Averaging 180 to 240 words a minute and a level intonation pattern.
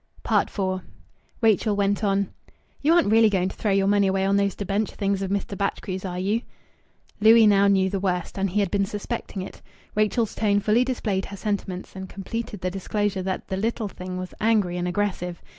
Yes: average, 195 wpm; narrow, 1.8 semitones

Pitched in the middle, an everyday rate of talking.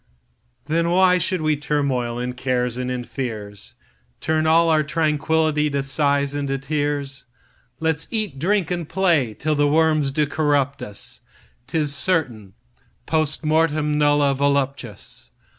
No: medium, 145 Hz; slow, 125 wpm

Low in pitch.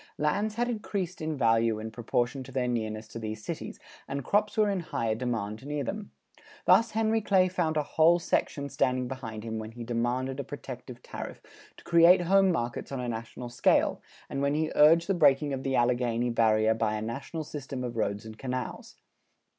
Yes: low, 130 Hz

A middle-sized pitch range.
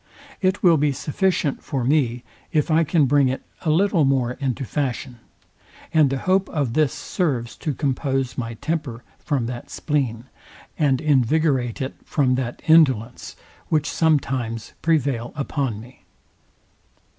Yes: average, 3.9 semitones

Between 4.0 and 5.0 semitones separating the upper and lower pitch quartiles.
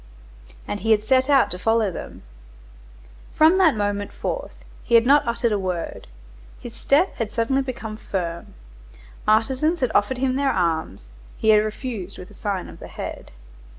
Yes: average, 4.5 semitones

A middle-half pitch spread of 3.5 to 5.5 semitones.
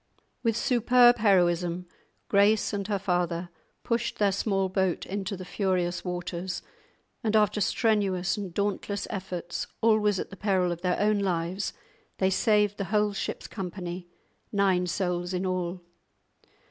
No: narrow, 2.6 semitones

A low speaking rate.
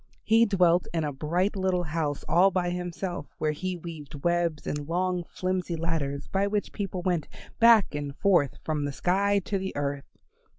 No: average, 175 wpm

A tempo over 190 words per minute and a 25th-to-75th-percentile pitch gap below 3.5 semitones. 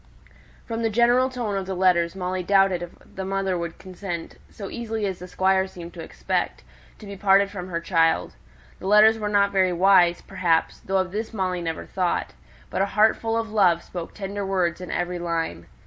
Yes: average, 200 wpm; narrow, 2.5 semitones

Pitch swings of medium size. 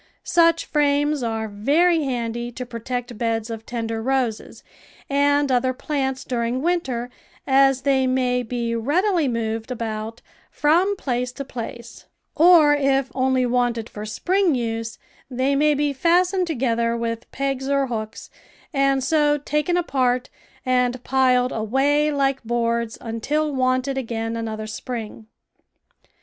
Yes: average, 3.4 semitones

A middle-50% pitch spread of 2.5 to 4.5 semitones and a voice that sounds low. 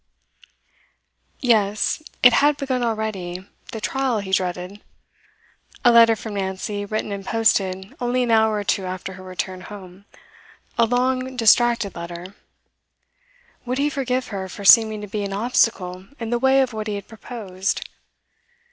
No: average, 4.0 semitones; high, 215 Hz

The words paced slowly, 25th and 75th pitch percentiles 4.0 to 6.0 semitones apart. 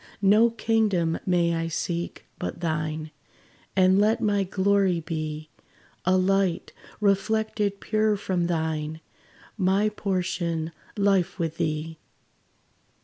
No: slow, 105 wpm; average, 3.6 semitones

